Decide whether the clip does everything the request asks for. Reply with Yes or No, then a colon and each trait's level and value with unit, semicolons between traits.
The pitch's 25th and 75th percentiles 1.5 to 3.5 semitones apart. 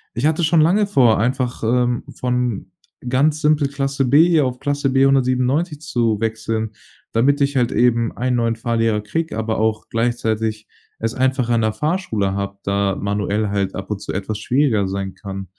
No: average, 4.1 semitones